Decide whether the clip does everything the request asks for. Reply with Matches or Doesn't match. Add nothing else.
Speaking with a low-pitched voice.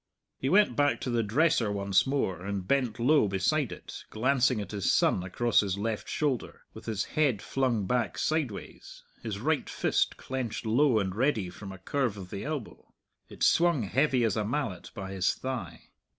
Matches